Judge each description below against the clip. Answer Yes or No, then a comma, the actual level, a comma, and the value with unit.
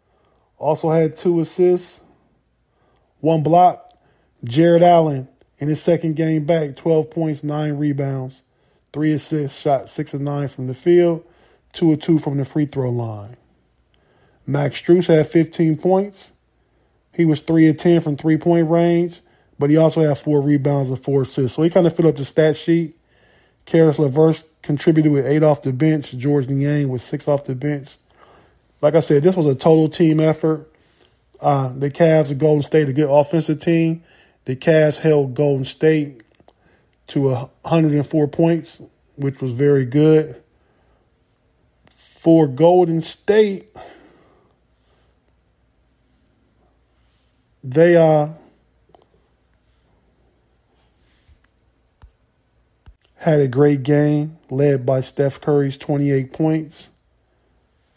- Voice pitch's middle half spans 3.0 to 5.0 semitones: No, narrow, 2.5 semitones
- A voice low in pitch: No, medium, 150 Hz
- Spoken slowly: Yes, slow, 130 wpm